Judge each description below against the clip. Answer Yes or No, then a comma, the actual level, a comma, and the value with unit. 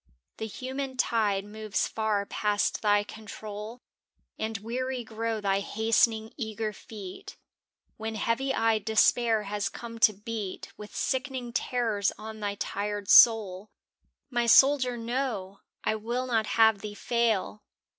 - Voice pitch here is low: No, high, 220 Hz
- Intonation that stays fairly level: Yes, narrow, 2.2 semitones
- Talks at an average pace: No, slow, 130 wpm